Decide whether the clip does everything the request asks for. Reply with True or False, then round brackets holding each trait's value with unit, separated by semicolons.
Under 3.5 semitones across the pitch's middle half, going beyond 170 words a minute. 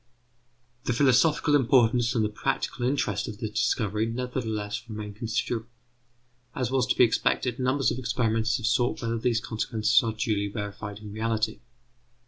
False (2.5 semitones; 150 wpm)